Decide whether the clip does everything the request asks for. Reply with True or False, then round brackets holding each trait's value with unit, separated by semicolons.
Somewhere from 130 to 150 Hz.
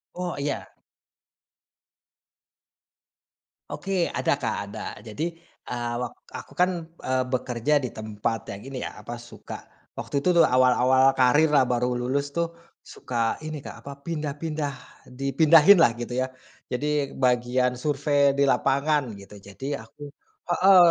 True (135 Hz)